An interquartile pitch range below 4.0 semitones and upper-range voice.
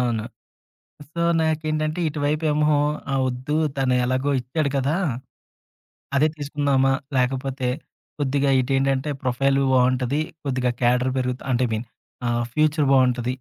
No: average, 2.7 semitones; low, 135 Hz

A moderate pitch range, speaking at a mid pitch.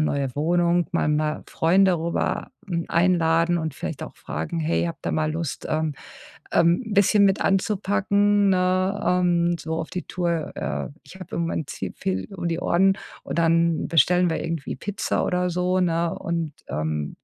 No: narrow, 2.3 semitones; medium, 170 Hz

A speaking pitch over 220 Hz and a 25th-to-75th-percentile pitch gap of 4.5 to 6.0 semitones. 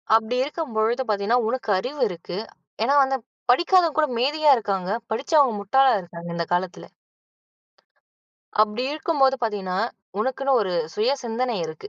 Yes: high, 240 Hz; average, 5.1 semitones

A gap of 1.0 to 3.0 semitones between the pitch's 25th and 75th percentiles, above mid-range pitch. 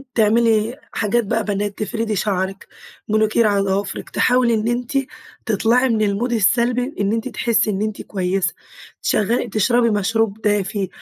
Yes: narrow, 2.6 semitones; high, 215 Hz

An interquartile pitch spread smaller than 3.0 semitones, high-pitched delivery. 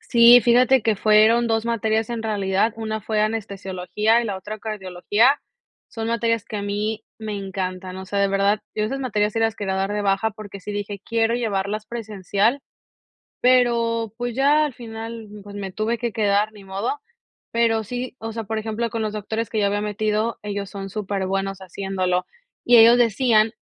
Yes: narrow, 2.4 semitones; high, 215 Hz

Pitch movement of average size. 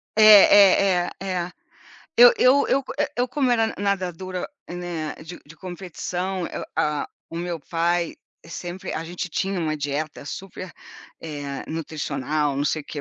Yes: average, 3.6 semitones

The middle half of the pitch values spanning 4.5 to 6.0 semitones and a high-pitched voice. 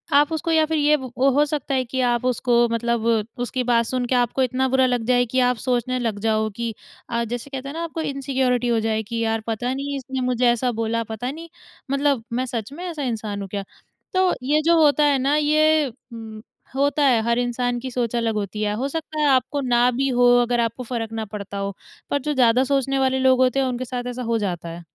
No: average, 3.0 semitones; very high, 250 Hz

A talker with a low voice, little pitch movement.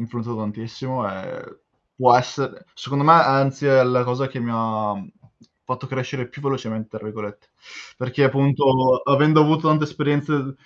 No: low, 130 Hz; average, 3.1 semitones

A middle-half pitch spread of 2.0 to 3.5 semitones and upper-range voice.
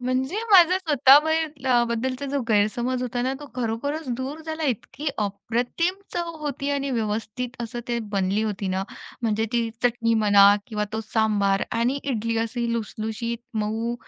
No: average, 4.0 semitones; high, 240 Hz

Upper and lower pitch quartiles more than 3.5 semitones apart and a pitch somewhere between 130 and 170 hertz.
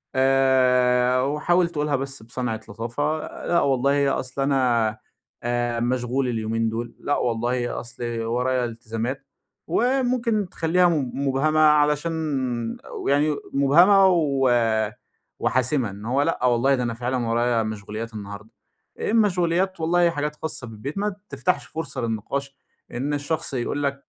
Yes: average, 4.0 semitones; low, 135 Hz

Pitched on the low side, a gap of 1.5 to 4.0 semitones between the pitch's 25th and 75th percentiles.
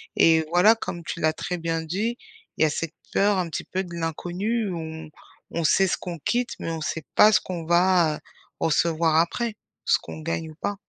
No: medium, 170 Hz; average, 2.8 semitones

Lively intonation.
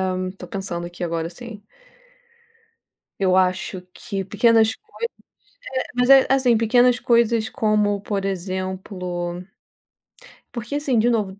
No: average, 4.2 semitones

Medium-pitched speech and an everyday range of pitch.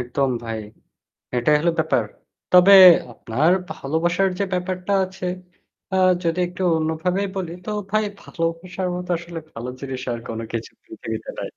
Yes: medium, 170 Hz; average, 4.7 semitones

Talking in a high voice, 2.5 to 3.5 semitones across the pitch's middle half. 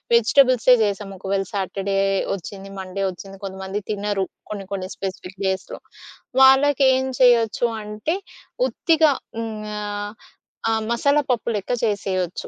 No: high, 205 Hz; average, 4.0 semitones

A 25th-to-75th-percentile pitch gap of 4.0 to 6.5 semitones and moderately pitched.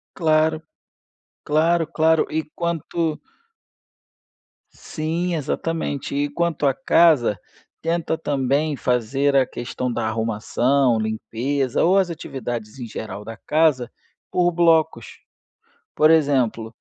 Yes: average, 5.0 semitones; medium, 145 Hz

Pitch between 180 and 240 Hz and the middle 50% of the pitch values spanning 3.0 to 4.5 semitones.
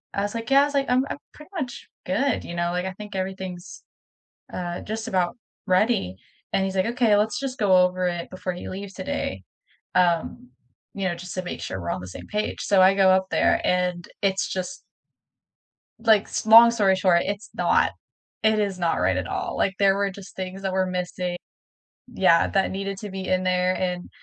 No: high, 190 Hz; narrow, 2.4 semitones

